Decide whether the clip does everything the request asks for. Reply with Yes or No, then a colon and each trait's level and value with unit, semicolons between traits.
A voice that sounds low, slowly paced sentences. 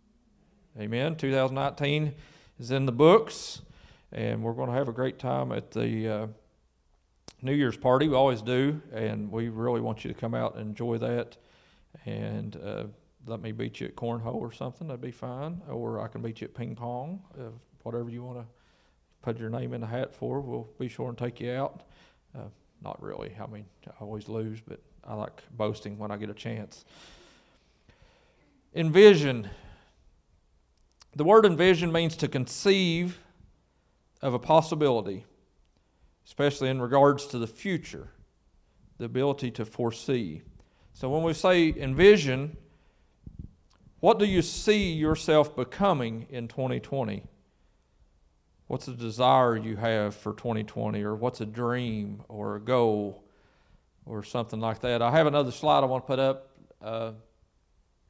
No: low, 120 Hz; average, 155 wpm